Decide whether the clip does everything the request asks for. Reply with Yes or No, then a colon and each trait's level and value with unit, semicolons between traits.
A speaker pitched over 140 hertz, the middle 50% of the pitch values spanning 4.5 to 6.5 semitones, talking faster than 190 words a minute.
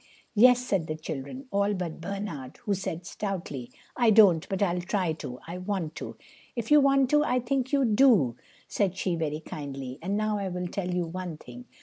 Yes: high, 190 Hz; average, 5.1 semitones; average, 200 wpm